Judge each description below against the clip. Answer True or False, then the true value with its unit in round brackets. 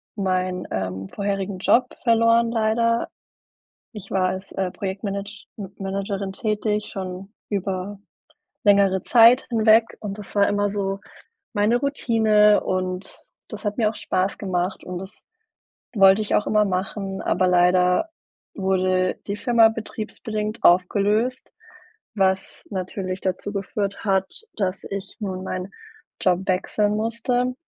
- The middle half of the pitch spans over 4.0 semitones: False (2.4 semitones)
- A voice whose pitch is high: True (200 Hz)